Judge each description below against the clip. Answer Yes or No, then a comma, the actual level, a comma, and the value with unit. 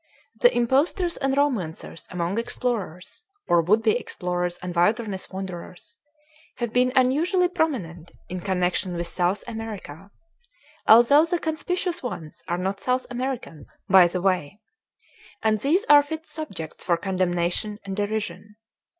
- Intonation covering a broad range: Yes, wide, 6.7 semitones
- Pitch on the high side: Yes, high, 210 Hz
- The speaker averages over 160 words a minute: No, slow, 135 wpm